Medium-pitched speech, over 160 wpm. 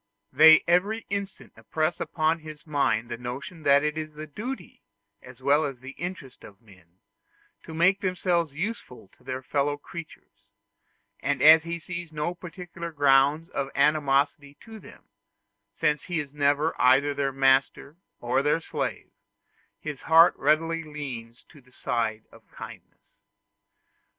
No: medium, 150 Hz; average, 145 wpm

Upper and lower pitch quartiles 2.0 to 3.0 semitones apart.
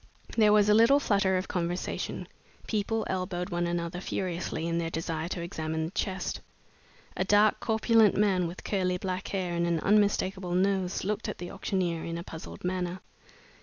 Yes: average, 2.7 semitones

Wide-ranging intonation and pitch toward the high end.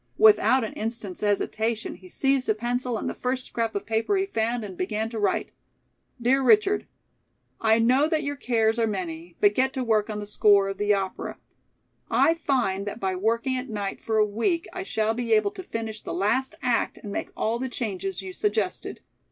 No: average, 3.6 semitones; high, 225 Hz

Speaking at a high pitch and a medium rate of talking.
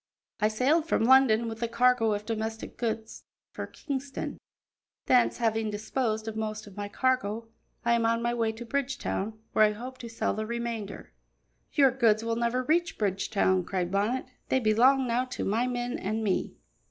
Yes: high, 230 Hz; average, 175 wpm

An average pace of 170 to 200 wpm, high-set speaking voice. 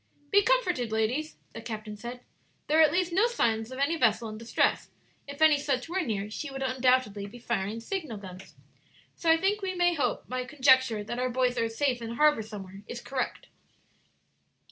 Yes: average, 190 wpm; very high, 250 Hz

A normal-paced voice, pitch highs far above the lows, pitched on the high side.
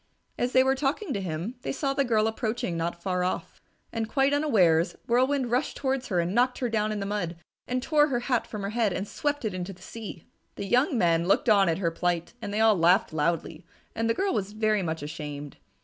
No: fast, 230 wpm; wide, 6.1 semitones; high, 215 Hz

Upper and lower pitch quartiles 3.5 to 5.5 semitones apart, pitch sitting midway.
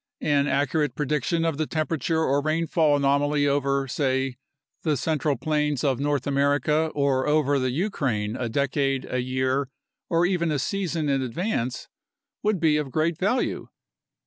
No: narrow, 2.6 semitones; medium, 145 Hz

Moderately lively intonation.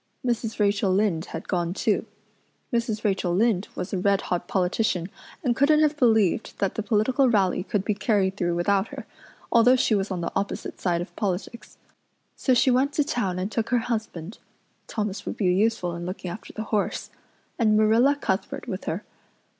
Yes: average, 3.8 semitones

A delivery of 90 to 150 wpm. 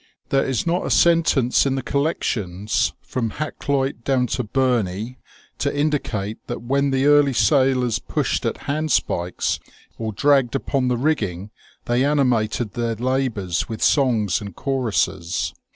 Yes: average, 145 wpm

